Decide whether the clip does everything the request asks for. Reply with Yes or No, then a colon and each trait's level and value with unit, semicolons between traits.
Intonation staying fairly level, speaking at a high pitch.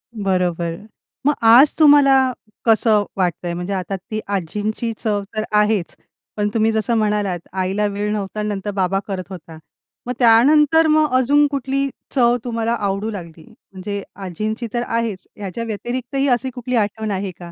No: average, 3.7 semitones; high, 210 Hz